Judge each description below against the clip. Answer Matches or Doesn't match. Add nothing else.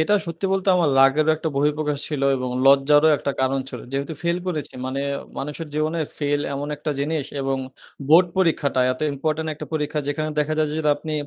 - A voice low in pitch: Doesn't match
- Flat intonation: Matches